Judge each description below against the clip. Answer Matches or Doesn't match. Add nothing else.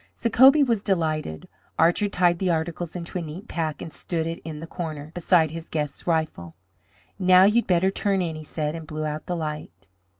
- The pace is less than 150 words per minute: Doesn't match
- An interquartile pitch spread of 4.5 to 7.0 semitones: Doesn't match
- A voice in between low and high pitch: Matches